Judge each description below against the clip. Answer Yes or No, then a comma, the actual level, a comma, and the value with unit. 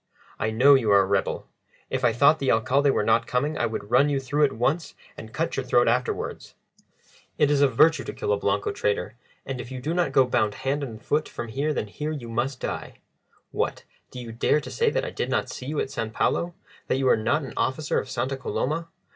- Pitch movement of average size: Yes, average, 4.2 semitones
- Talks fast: Yes, fast, 240 wpm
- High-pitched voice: No, low, 130 Hz